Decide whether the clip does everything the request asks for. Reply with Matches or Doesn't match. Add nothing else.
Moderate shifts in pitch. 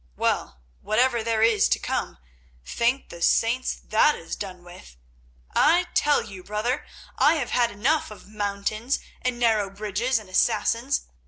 Matches